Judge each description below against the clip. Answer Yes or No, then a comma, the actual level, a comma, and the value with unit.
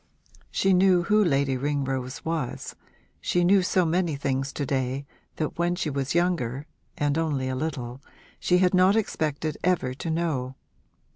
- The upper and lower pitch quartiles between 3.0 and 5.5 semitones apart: Yes, average, 4.7 semitones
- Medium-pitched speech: Yes, medium, 155 Hz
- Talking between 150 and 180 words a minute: Yes, average, 155 wpm